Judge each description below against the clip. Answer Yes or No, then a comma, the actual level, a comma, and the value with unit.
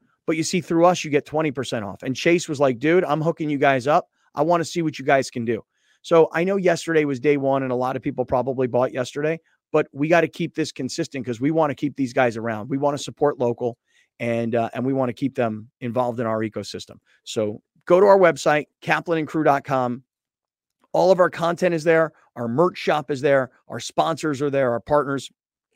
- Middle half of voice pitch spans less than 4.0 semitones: No, average, 4.3 semitones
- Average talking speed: No, fast, 230 wpm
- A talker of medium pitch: Yes, medium, 145 Hz